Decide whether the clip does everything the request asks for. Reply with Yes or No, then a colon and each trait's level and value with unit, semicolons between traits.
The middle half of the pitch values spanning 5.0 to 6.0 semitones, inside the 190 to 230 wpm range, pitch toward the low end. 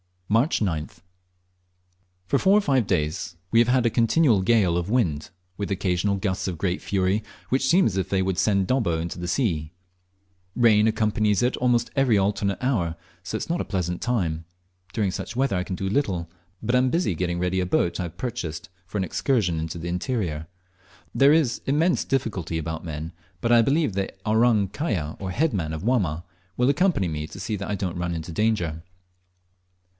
Yes: wide, 5.5 semitones; average, 195 wpm; low, 100 Hz